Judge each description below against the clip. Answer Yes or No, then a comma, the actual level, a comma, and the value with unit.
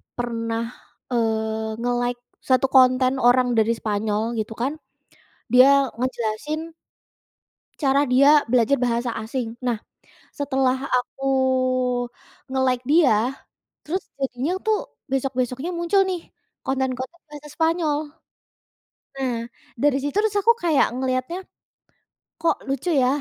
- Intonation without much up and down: No, average, 3.1 semitones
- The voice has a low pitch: No, very high, 260 Hz